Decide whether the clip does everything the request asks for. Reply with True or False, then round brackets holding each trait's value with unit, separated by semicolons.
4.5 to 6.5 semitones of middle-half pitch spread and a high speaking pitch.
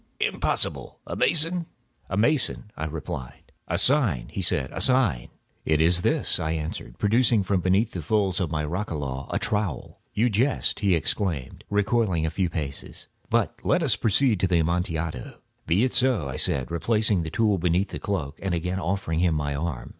False (5.0 semitones; 90 Hz)